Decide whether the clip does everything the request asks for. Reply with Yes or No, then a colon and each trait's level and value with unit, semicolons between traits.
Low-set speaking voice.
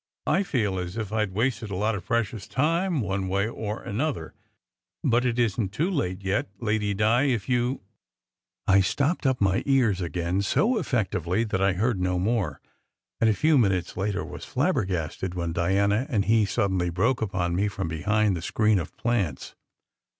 Yes: low, 105 Hz